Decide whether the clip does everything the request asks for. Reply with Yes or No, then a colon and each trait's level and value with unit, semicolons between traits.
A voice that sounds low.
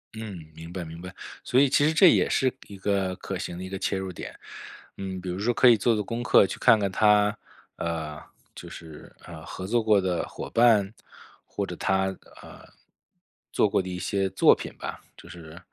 Yes: very low, 95 Hz